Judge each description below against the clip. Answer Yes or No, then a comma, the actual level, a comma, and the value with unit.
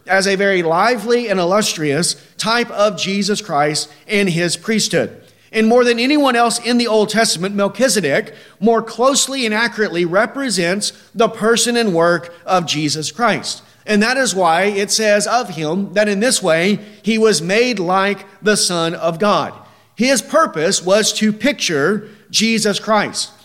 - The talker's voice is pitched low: No, high, 210 Hz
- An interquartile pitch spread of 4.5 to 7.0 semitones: No, average, 3.8 semitones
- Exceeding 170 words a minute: No, average, 160 wpm